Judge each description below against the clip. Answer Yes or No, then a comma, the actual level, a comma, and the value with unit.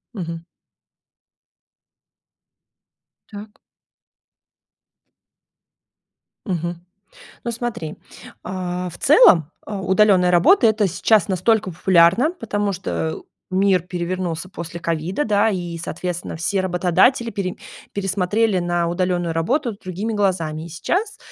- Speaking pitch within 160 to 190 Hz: Yes, medium, 185 Hz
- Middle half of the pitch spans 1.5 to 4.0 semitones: Yes, average, 3.4 semitones